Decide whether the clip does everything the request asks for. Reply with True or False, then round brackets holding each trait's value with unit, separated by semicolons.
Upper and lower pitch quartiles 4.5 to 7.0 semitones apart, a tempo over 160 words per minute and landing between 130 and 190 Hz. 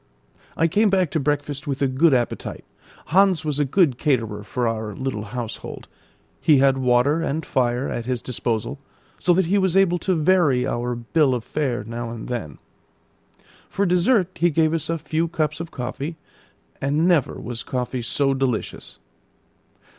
True (5.1 semitones; 170 wpm; 140 Hz)